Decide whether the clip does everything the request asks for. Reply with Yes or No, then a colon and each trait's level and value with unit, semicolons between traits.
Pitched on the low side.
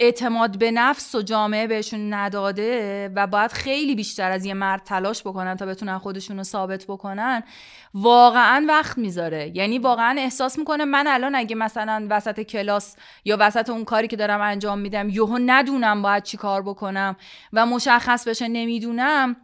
No: high, 215 Hz